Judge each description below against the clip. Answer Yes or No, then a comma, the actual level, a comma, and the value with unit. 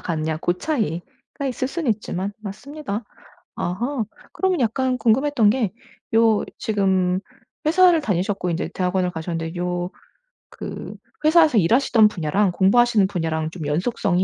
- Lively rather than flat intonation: Yes, wide, 6.0 semitones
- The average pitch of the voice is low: No, high, 205 Hz